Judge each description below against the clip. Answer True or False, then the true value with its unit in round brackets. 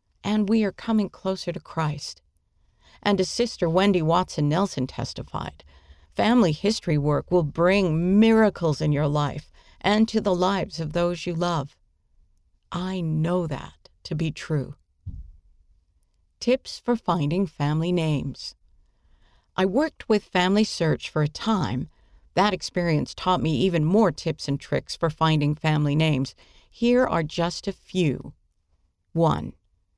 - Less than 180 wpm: True (140 wpm)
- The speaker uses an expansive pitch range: True (5.7 semitones)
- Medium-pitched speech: True (165 Hz)